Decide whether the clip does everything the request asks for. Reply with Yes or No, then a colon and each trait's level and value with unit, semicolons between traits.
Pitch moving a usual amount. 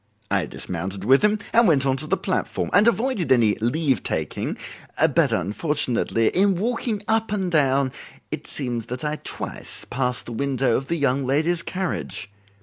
No: wide, 6.8 semitones